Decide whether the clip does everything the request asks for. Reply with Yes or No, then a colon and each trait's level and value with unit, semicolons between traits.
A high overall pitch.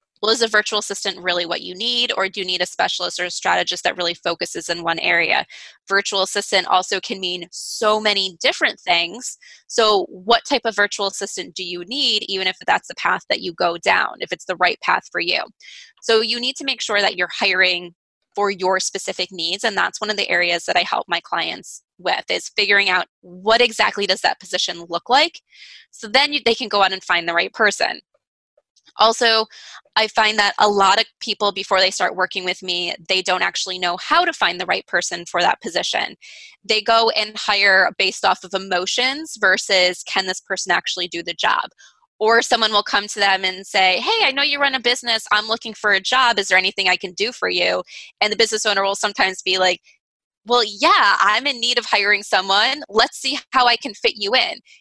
Yes: high, 200 Hz